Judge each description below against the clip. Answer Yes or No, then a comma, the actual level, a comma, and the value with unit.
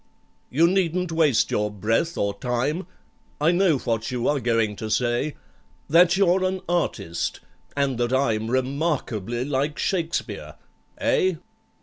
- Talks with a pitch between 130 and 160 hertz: Yes, medium, 140 Hz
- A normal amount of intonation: No, wide, 6.3 semitones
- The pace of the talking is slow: Yes, slow, 130 wpm